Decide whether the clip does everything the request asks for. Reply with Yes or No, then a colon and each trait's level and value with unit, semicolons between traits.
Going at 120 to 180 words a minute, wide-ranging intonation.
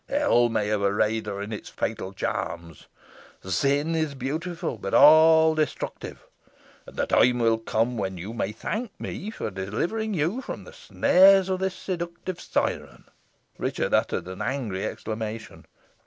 Yes: average, 150 wpm; wide, 8.2 semitones